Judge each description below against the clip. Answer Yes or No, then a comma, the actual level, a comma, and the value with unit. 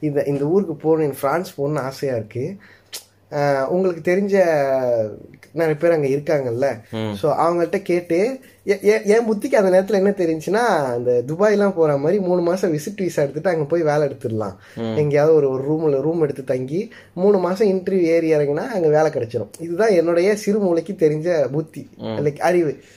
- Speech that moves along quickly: Yes, fast, 155 wpm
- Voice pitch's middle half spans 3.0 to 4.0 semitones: No, average, 4.8 semitones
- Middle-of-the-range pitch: Yes, medium, 160 Hz